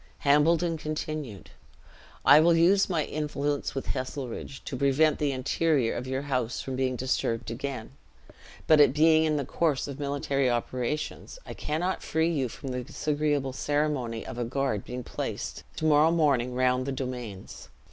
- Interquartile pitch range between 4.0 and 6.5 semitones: No, average, 3.2 semitones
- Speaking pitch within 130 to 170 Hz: Yes, medium, 140 Hz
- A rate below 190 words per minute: Yes, average, 160 wpm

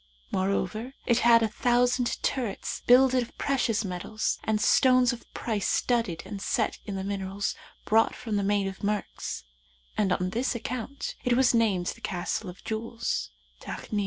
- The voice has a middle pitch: No, high, 220 Hz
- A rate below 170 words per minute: Yes, average, 160 wpm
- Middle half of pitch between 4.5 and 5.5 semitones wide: No, average, 3.6 semitones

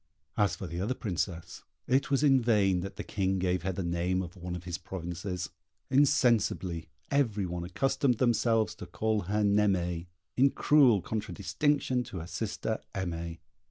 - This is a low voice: Yes, very low, 95 Hz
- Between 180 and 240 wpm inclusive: No, average, 160 wpm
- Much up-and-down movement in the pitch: No, average, 5.0 semitones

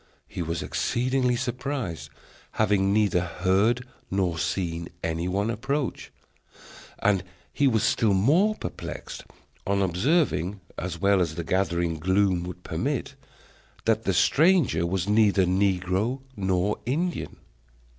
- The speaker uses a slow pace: Yes, slow, 120 wpm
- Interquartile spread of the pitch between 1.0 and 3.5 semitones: No, wide, 5.4 semitones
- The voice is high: No, low, 100 Hz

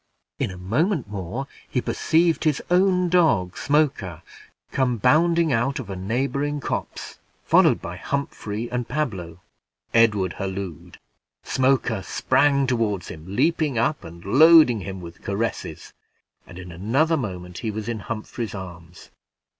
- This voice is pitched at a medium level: No, low, 115 Hz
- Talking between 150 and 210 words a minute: No, slow, 135 wpm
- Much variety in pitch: Yes, wide, 7.4 semitones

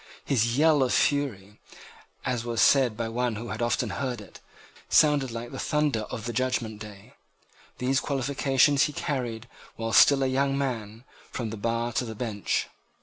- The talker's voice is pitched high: No, low, 120 Hz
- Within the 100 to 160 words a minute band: No, average, 170 wpm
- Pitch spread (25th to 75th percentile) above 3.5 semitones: No, average, 3.2 semitones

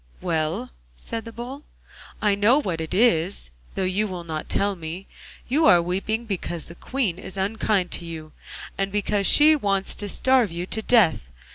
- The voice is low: No, high, 195 Hz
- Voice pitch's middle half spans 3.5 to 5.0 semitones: Yes, average, 4.6 semitones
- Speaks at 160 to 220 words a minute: Yes, average, 175 wpm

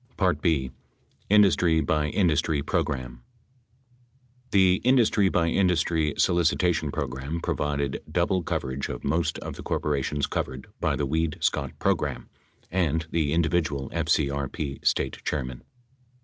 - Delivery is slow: Yes, slow, 120 wpm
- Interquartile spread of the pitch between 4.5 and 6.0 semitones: No, average, 3.7 semitones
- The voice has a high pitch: No, very low, 75 Hz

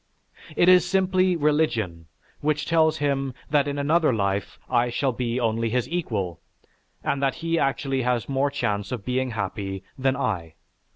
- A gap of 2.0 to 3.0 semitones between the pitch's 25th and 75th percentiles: No, average, 5.1 semitones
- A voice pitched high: No, low, 135 Hz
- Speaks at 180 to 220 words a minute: No, average, 160 wpm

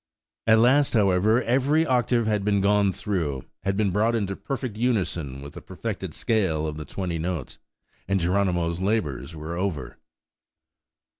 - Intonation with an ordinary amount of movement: Yes, average, 4.7 semitones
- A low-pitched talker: Yes, low, 100 Hz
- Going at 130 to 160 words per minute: Yes, average, 150 wpm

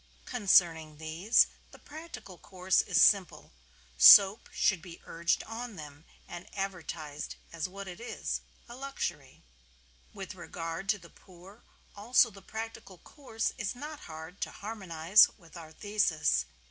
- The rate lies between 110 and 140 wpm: Yes, slow, 135 wpm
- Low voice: No, high, 190 Hz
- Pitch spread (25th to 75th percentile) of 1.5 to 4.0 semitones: No, average, 4.5 semitones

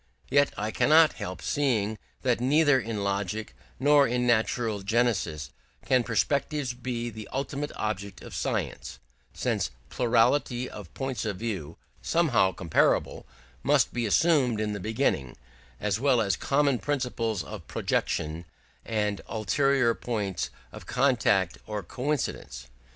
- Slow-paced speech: Yes, slow, 130 wpm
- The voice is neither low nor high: No, low, 115 Hz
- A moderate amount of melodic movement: Yes, average, 4.7 semitones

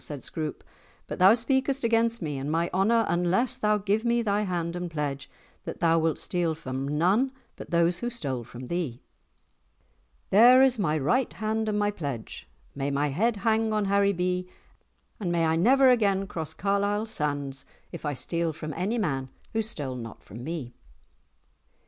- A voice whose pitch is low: No, medium, 180 Hz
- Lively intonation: Yes, wide, 6.4 semitones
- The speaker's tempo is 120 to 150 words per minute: No, average, 170 wpm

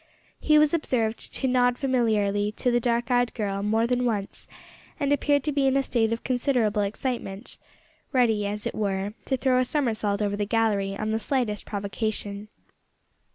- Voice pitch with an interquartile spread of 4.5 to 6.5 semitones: No, average, 3.6 semitones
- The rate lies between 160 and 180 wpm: Yes, average, 175 wpm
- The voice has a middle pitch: No, high, 225 Hz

